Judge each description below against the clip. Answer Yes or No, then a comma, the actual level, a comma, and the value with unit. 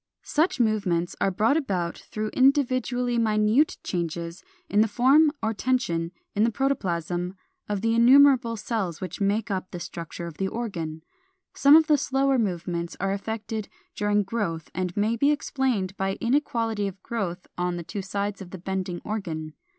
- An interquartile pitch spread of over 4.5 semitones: Yes, average, 4.9 semitones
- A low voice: No, high, 205 Hz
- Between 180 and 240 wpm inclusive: No, average, 165 wpm